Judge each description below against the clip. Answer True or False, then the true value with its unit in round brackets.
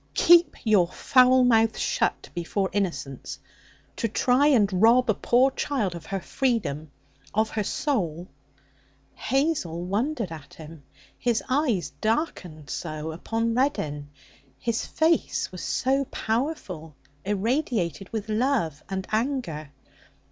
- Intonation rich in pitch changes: True (7.1 semitones)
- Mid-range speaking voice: False (215 Hz)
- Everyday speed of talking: False (120 wpm)